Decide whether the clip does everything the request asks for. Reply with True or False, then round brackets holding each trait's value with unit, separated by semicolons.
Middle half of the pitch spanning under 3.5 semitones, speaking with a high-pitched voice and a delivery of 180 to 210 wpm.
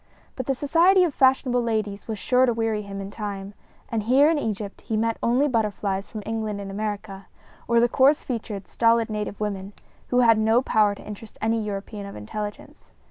True (2.9 semitones; 220 Hz; 190 wpm)